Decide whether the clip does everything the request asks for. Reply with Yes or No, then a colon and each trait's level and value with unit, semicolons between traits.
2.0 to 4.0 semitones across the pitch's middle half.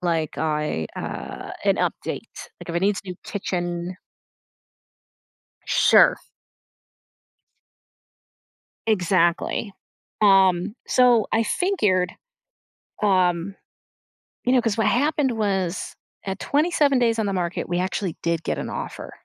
No: average, 4.4 semitones